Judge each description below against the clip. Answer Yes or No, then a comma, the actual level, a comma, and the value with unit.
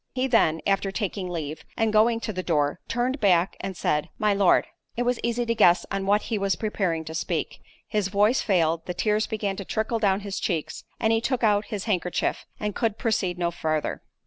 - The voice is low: No, high, 200 Hz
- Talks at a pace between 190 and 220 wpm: Yes, average, 200 wpm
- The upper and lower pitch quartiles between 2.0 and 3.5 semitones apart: No, average, 3.9 semitones